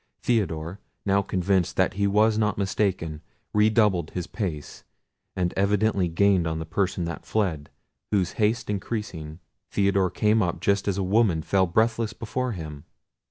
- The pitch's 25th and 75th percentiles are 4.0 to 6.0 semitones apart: No, average, 3.4 semitones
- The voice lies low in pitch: Yes, low, 100 Hz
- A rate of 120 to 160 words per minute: Yes, average, 150 wpm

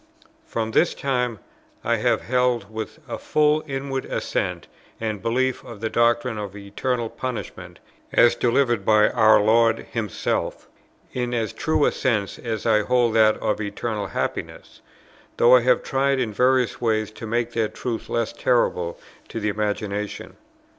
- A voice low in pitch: Yes, low, 115 Hz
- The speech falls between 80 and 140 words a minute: No, average, 150 wpm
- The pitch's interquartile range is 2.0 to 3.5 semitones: Yes, average, 2.7 semitones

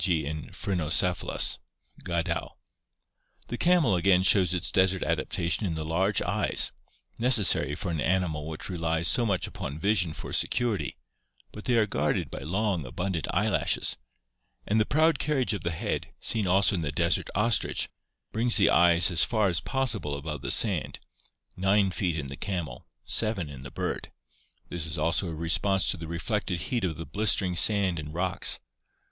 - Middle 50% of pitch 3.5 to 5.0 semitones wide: Yes, average, 4.3 semitones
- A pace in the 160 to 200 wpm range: Yes, average, 170 wpm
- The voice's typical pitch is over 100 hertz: No, very low, 90 Hz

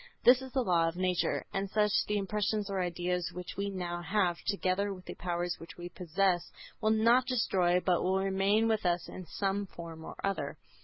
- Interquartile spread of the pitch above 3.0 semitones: No, average, 2.7 semitones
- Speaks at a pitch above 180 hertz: Yes, high, 190 Hz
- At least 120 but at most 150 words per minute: No, fast, 205 wpm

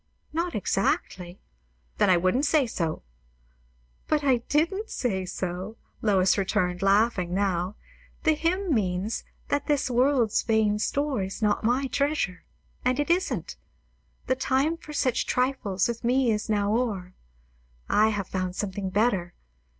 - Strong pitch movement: Yes, wide, 6.3 semitones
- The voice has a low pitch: No, high, 220 Hz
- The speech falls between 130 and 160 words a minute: Yes, average, 140 wpm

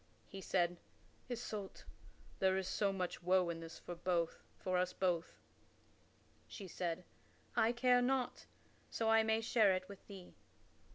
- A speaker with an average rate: No, slow, 130 wpm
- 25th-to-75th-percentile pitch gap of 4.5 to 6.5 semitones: No, average, 3.7 semitones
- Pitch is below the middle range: No, high, 190 Hz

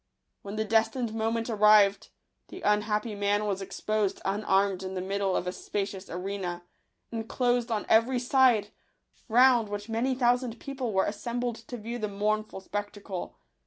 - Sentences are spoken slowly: No, average, 150 wpm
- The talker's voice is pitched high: Yes, high, 215 Hz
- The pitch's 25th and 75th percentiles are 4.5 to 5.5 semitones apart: No, average, 2.8 semitones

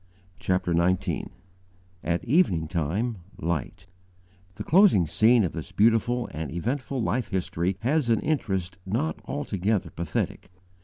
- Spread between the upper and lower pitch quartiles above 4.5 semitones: Yes, wide, 5.6 semitones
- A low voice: Yes, very low, 95 Hz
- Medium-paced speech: No, slow, 120 wpm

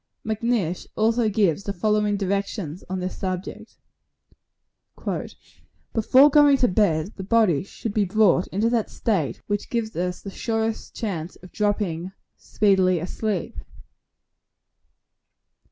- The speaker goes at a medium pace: No, slow, 120 wpm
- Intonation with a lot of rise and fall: No, average, 3.3 semitones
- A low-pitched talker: No, high, 200 Hz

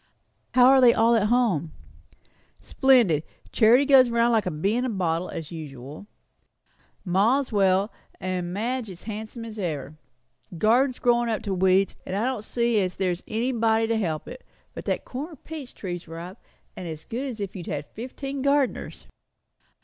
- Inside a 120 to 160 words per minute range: No, average, 170 wpm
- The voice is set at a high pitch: Yes, high, 220 Hz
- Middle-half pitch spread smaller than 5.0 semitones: No, average, 5.3 semitones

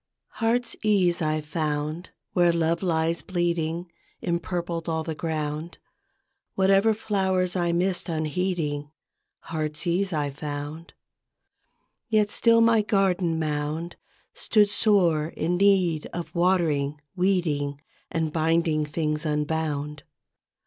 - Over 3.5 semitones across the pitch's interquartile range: No, average, 3.1 semitones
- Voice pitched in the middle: Yes, medium, 170 Hz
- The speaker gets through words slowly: Yes, slow, 100 wpm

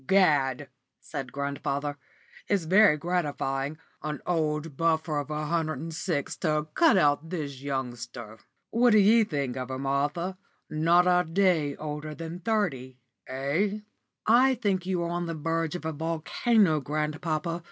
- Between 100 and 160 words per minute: Yes, average, 150 wpm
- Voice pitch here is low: No, medium, 155 Hz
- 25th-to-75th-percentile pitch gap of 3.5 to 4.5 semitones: Yes, average, 3.8 semitones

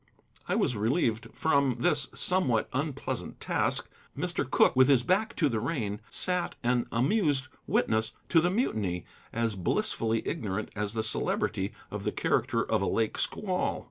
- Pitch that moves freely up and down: Yes, wide, 6.3 semitones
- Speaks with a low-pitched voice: Yes, low, 125 Hz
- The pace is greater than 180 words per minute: No, average, 155 wpm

